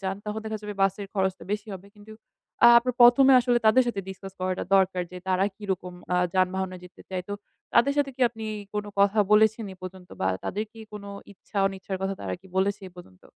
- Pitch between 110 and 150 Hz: No, high, 200 Hz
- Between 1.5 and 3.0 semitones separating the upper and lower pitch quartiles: Yes, narrow, 2.6 semitones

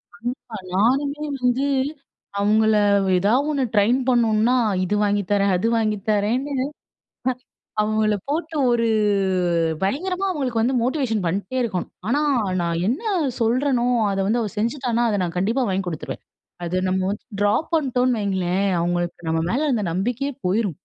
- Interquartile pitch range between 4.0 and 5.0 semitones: Yes, average, 4.5 semitones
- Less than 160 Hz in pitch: No, high, 225 Hz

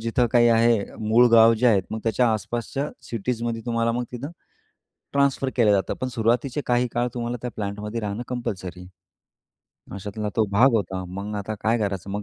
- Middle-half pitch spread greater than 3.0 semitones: No, average, 2.7 semitones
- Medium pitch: No, low, 115 Hz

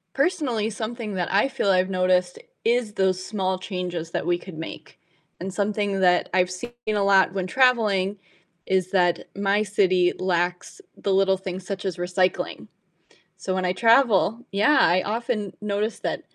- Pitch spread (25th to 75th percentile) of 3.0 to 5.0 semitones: No, narrow, 2.5 semitones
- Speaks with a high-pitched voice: Yes, high, 195 Hz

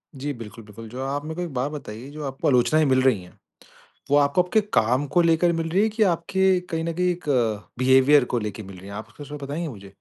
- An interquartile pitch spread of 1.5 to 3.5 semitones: No, average, 5.3 semitones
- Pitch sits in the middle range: Yes, medium, 145 Hz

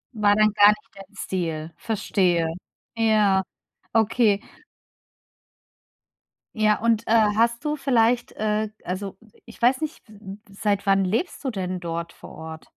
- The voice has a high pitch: Yes, high, 210 Hz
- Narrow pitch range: No, average, 3.0 semitones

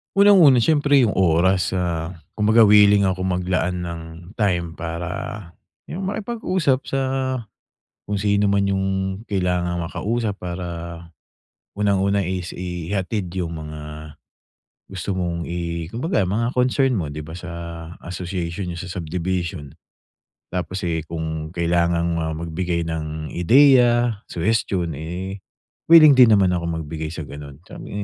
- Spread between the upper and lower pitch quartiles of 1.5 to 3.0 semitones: No, average, 3.6 semitones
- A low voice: Yes, very low, 90 Hz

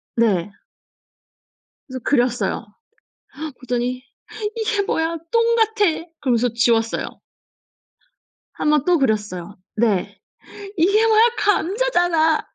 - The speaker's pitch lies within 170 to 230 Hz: No, very high, 300 Hz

